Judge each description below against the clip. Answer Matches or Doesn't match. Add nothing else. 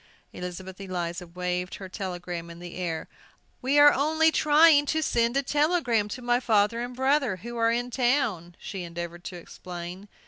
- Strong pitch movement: Matches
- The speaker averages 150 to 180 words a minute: Matches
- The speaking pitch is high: Matches